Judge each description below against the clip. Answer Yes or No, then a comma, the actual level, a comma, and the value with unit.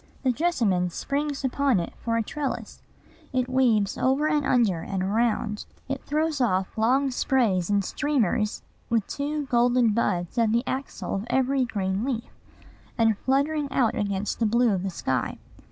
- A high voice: Yes, high, 235 Hz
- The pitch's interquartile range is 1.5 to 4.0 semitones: No, average, 4.8 semitones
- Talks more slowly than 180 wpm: Yes, average, 160 wpm